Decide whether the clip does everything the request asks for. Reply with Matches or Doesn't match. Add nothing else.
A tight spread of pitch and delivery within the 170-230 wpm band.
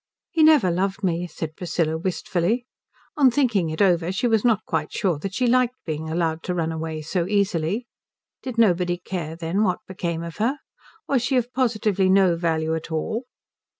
Doesn't match